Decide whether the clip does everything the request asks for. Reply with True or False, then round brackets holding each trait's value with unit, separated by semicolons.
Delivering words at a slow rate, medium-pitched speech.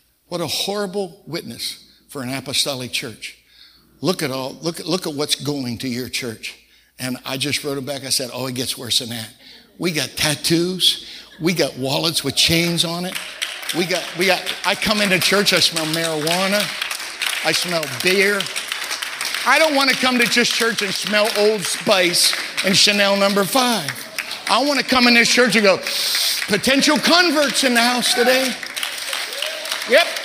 False (180 wpm; 180 Hz)